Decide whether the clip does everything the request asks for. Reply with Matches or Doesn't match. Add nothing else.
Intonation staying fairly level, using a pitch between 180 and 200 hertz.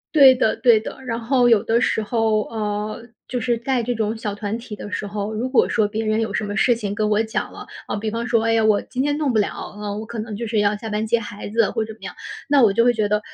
Doesn't match